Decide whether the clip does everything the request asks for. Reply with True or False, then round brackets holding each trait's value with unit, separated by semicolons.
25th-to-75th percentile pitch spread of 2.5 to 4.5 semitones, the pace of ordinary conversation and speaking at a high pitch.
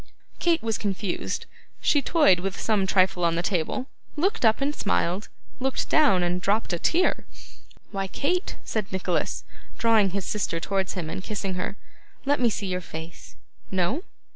False (4.9 semitones; 165 wpm; 195 Hz)